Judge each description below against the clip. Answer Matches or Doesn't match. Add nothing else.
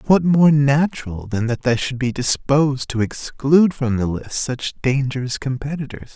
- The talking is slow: Doesn't match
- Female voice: Doesn't match